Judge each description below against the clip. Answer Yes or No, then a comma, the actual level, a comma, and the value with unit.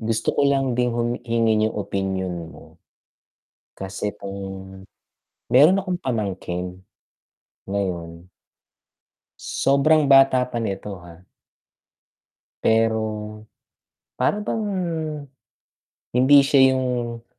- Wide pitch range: Yes, wide, 5.7 semitones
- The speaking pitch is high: No, low, 115 Hz